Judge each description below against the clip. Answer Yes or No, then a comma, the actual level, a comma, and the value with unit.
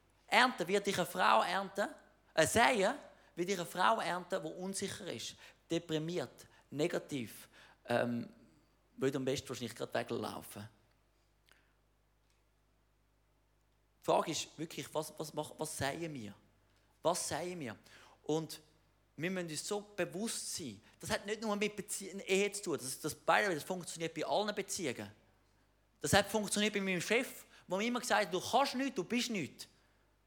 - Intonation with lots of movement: Yes, wide, 7.1 semitones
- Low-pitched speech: No, medium, 170 Hz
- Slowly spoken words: No, average, 155 wpm